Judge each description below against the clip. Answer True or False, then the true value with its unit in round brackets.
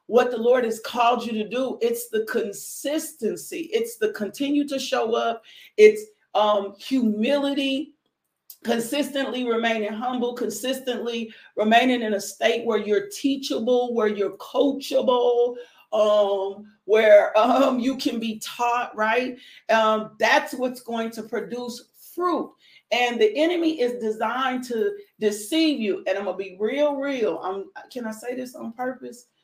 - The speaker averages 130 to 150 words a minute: True (145 wpm)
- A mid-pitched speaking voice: False (245 Hz)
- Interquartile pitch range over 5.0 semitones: False (4.6 semitones)